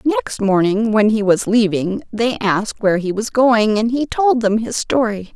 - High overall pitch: Yes, high, 220 Hz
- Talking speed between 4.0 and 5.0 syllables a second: Yes, 4.5 syllables/s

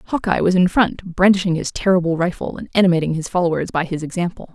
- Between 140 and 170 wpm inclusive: No, average, 200 wpm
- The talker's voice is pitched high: No, medium, 180 Hz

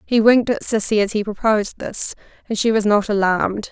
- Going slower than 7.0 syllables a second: Yes, 5.9 syllables/s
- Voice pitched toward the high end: Yes, high, 215 Hz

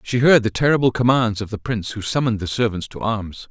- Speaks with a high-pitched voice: No, low, 115 Hz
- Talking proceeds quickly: Yes, fast, 240 wpm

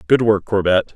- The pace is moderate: Yes, average, 190 wpm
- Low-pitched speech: Yes, low, 105 Hz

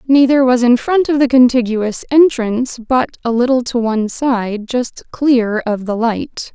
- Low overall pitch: No, high, 245 Hz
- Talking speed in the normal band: Yes, average, 175 wpm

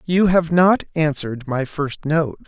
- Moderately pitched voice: Yes, medium, 155 Hz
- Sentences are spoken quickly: No, average, 170 wpm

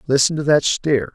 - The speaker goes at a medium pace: No, fast, 210 wpm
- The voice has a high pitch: No, medium, 140 Hz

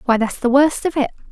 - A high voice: Yes, very high, 265 Hz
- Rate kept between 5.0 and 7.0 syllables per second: Yes, 6.1 syllables/s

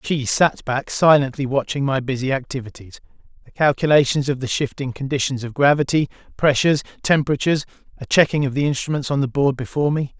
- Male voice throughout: Yes, male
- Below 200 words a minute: Yes, average, 165 wpm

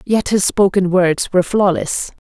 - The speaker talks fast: No, average, 160 wpm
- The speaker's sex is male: No, female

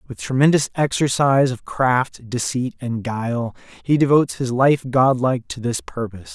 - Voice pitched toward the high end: No, low, 125 Hz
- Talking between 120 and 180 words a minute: Yes, average, 150 wpm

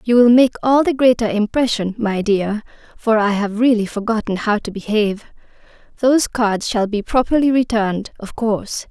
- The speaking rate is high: No, average, 170 wpm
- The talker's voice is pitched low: No, high, 225 Hz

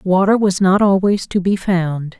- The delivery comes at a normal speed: Yes, average, 190 wpm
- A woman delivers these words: Yes, female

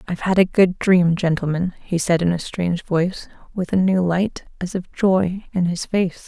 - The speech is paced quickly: Yes, fast, 210 wpm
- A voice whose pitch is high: No, medium, 180 Hz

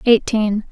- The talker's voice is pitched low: No, high, 220 Hz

